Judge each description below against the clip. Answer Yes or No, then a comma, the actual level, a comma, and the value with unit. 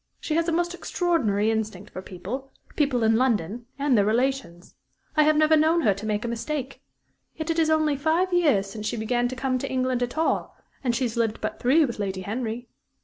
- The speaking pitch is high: Yes, very high, 250 Hz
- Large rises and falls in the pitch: Yes, wide, 5.8 semitones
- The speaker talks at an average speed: No, fast, 210 wpm